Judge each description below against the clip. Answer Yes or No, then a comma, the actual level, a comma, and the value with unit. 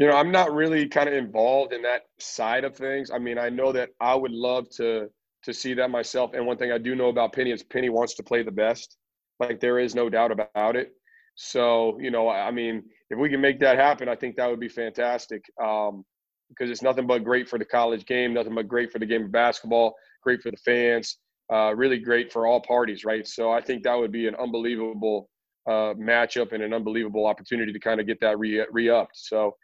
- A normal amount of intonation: No, narrow, 1.8 semitones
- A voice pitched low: Yes, low, 120 Hz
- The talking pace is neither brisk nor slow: No, fast, 235 wpm